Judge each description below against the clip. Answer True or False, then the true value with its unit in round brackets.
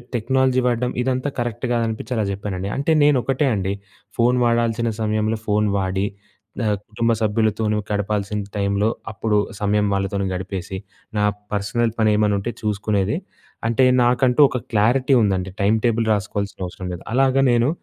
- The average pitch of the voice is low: True (110 Hz)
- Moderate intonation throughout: True (3.1 semitones)